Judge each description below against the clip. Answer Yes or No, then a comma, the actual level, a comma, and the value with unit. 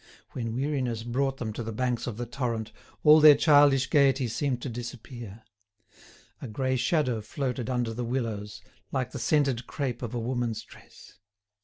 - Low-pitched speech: Yes, low, 125 Hz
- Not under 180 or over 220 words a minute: No, average, 165 wpm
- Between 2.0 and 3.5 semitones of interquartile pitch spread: Yes, average, 2.8 semitones